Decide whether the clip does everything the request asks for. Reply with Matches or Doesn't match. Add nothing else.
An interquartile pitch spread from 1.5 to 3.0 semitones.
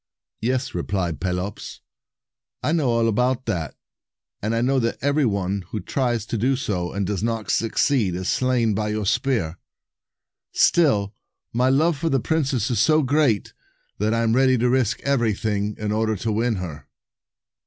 Doesn't match